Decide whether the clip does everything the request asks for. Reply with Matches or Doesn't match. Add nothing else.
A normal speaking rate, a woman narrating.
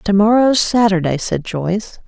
Matches